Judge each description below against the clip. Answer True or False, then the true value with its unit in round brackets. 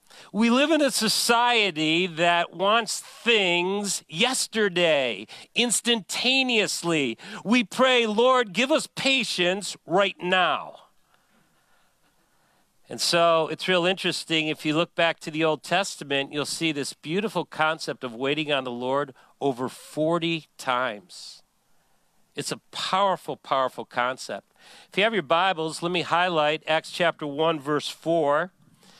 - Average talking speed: False (130 wpm)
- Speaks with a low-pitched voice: False (170 Hz)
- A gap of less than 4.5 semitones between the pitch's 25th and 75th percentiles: False (5.1 semitones)